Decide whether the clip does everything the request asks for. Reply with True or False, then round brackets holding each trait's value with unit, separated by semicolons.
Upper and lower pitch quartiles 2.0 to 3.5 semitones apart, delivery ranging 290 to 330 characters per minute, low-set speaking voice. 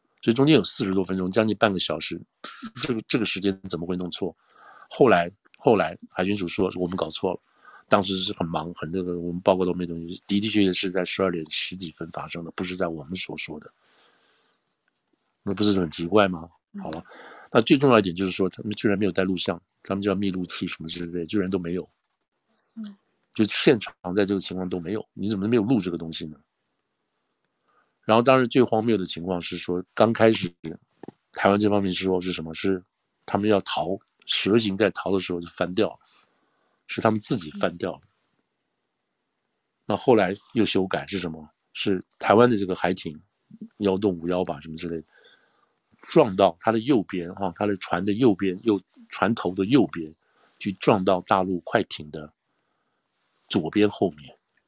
False (2.8 semitones; 275 characters per minute; 95 Hz)